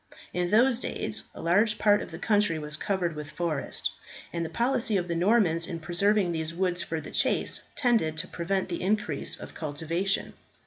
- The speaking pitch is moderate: Yes, medium, 180 Hz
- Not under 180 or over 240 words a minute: Yes, average, 185 wpm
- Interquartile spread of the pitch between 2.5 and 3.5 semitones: No, average, 4.0 semitones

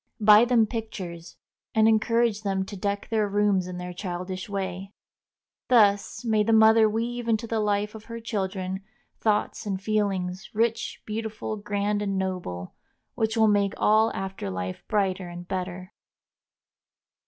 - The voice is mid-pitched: No, high, 205 Hz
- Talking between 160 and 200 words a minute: No, average, 145 wpm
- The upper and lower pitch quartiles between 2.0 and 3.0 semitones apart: Yes, average, 2.7 semitones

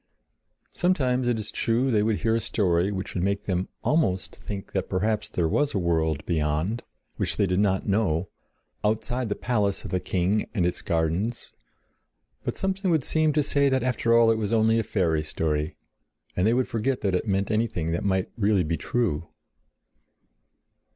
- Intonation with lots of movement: No, average, 4.6 semitones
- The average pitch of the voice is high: No, low, 105 Hz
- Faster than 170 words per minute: Yes, average, 185 wpm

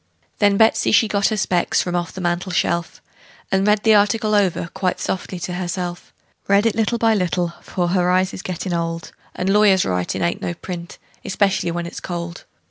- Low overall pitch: No, medium, 185 Hz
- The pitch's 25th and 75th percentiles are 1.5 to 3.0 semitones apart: Yes, average, 2.7 semitones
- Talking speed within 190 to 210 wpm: Yes, average, 200 wpm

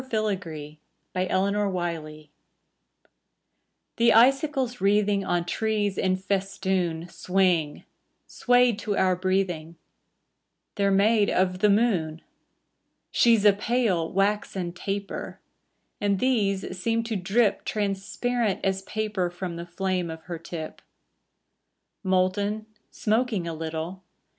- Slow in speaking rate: Yes, slow, 105 wpm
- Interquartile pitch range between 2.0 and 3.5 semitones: Yes, average, 3.1 semitones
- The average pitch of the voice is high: Yes, high, 195 Hz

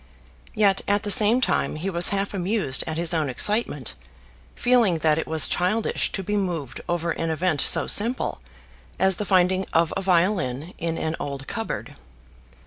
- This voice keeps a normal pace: Yes, average, 170 wpm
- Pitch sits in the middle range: Yes, medium, 180 Hz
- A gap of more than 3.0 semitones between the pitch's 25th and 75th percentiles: Yes, average, 4.2 semitones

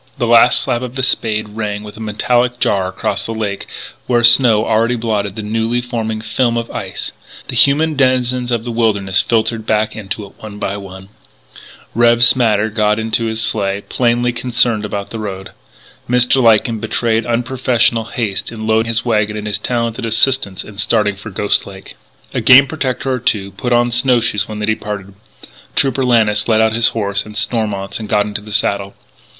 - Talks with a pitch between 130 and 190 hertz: No, low, 110 Hz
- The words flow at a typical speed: Yes, average, 185 wpm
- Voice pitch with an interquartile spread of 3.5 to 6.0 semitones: No, narrow, 2.4 semitones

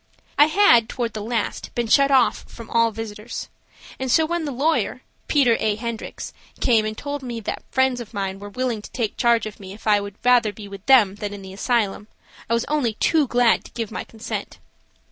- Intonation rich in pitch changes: No, average, 3.4 semitones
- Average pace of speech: No, fast, 215 wpm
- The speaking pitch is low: No, high, 230 Hz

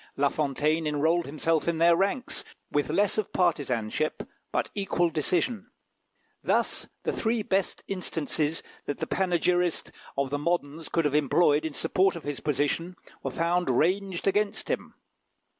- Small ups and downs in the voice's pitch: No, average, 3.7 semitones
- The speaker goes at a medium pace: Yes, average, 145 wpm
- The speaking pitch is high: No, medium, 165 Hz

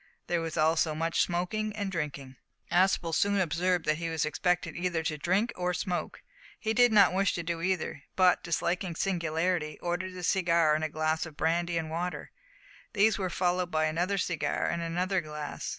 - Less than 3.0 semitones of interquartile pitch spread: Yes, narrow, 2.4 semitones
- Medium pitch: Yes, medium, 175 Hz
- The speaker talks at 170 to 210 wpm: Yes, average, 180 wpm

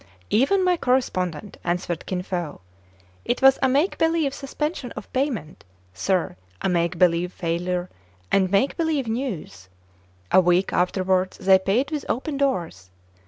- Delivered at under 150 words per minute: Yes, average, 140 wpm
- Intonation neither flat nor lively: No, wide, 7.4 semitones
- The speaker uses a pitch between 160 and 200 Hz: Yes, high, 190 Hz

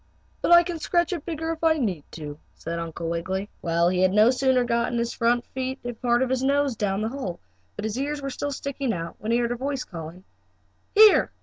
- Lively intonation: Yes, wide, 6.9 semitones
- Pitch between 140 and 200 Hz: No, high, 240 Hz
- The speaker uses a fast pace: Yes, fast, 230 wpm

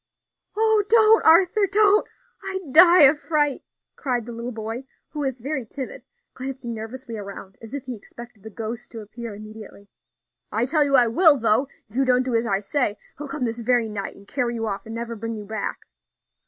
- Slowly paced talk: No, average, 200 wpm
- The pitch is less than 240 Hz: No, high, 245 Hz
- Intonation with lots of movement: No, average, 4.5 semitones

